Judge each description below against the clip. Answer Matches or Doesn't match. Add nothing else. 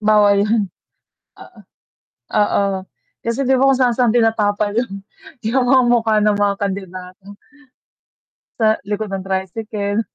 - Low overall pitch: Doesn't match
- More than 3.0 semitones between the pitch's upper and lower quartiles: Doesn't match